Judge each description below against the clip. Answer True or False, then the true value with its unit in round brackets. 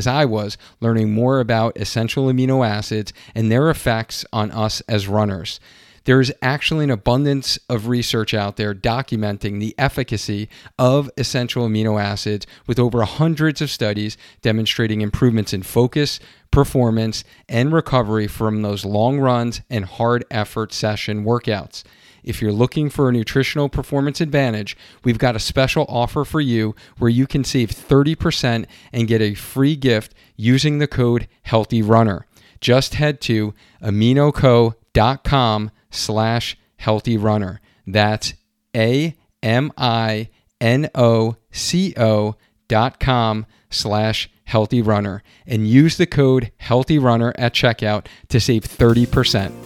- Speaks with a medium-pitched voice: False (115 Hz)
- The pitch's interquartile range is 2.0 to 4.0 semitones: True (3.3 semitones)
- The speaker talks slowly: True (125 wpm)